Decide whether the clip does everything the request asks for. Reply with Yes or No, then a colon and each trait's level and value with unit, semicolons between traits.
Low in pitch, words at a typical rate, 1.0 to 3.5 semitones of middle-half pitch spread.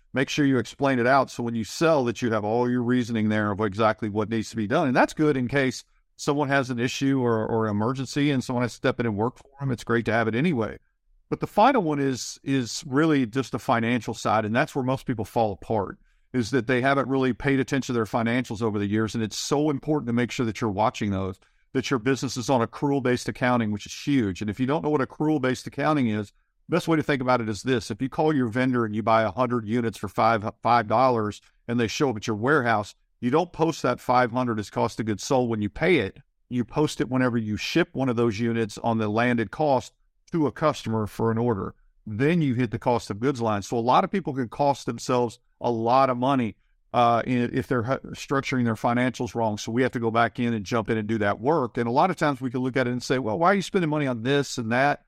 No: low, 125 Hz; fast, 265 wpm; average, 3.1 semitones